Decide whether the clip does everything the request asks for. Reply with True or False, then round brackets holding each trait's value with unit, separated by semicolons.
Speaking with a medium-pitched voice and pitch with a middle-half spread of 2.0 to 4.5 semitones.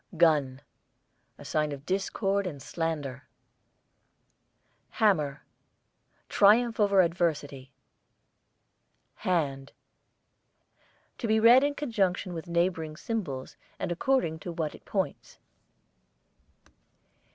False (170 Hz; 5.1 semitones)